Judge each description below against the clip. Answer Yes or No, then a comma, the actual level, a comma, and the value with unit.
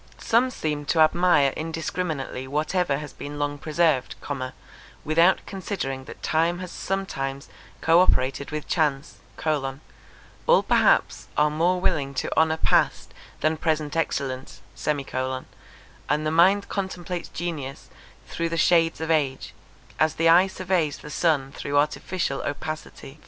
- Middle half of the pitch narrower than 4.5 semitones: Yes, average, 3.3 semitones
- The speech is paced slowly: Yes, slow, 130 wpm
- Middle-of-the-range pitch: Yes, medium, 155 Hz